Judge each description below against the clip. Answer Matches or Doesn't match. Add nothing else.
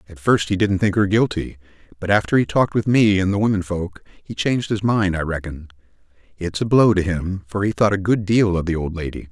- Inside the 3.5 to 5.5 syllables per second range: Doesn't match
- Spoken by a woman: Doesn't match